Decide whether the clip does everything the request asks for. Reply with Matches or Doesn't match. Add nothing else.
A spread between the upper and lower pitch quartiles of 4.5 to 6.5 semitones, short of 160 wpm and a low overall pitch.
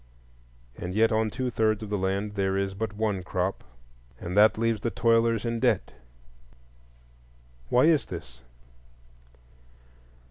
Doesn't match